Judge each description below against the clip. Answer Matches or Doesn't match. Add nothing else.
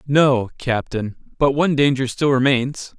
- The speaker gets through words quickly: Doesn't match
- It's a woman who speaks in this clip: Doesn't match